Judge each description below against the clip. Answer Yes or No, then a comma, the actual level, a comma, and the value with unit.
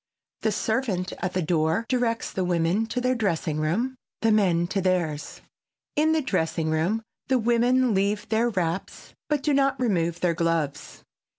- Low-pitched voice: No, high, 200 Hz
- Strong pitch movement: Yes, wide, 6.1 semitones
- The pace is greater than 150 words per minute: Yes, average, 165 wpm